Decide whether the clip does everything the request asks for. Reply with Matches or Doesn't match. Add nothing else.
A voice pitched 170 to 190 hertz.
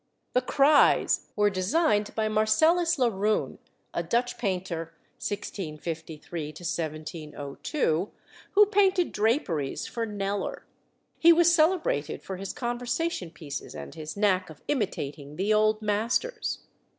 Doesn't match